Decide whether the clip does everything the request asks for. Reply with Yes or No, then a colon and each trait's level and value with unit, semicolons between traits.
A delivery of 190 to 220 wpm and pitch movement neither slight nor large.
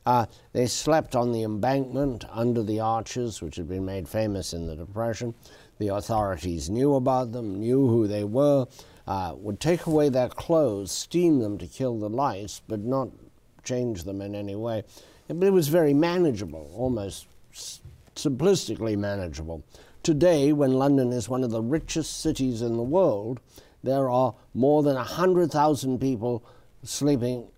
No: average, 160 wpm; average, 4.7 semitones